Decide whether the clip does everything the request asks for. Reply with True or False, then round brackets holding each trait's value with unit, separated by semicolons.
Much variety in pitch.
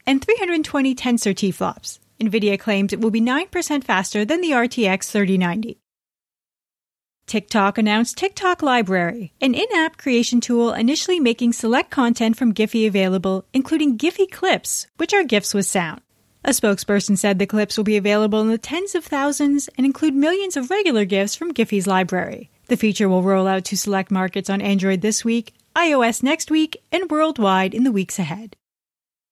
True (6.3 semitones)